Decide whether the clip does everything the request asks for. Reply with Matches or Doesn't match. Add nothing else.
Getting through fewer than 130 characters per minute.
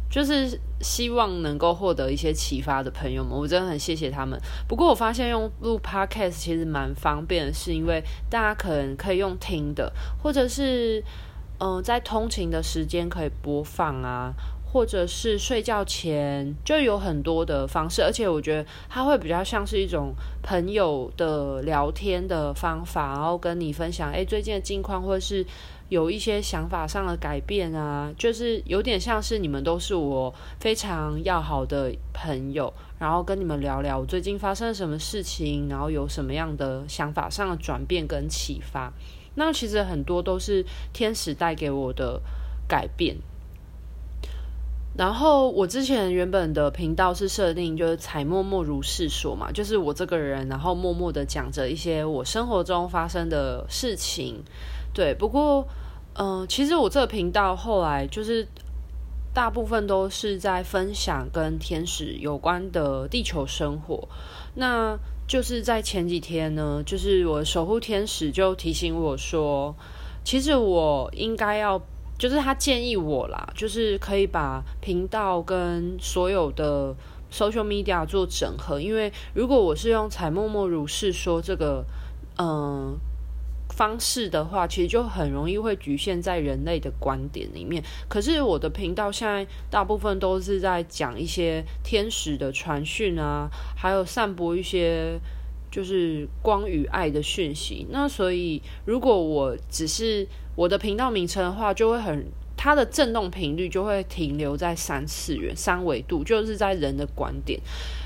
Doesn't match